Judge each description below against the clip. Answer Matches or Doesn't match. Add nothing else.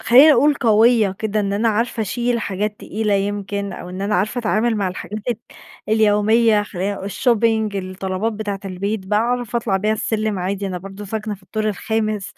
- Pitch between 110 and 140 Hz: Doesn't match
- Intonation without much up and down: Matches